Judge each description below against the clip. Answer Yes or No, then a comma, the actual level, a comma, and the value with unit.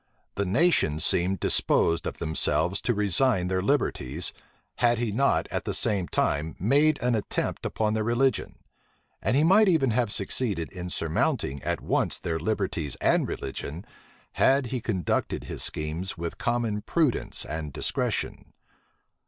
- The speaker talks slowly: No, average, 145 wpm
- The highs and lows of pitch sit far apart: Yes, wide, 6.7 semitones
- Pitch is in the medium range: No, low, 100 Hz